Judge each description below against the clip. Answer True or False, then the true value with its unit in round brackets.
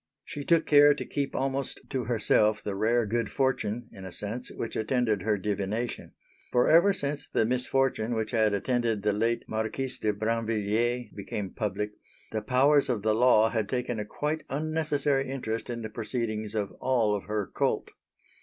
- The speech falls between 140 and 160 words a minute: False (175 wpm)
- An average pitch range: True (3.6 semitones)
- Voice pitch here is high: False (115 Hz)